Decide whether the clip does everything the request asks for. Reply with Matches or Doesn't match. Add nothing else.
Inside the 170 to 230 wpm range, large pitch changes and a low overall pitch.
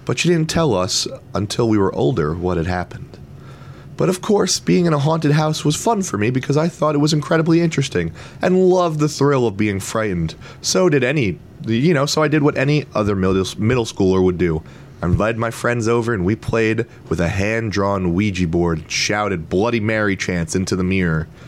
Matches